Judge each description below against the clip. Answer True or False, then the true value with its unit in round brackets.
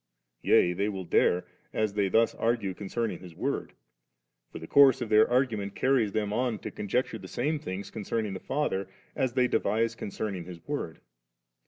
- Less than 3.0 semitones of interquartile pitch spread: False (3.8 semitones)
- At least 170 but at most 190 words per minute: True (175 wpm)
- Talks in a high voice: False (110 Hz)